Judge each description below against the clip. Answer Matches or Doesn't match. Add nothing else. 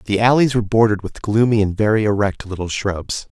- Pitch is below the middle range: Matches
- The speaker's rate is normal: Matches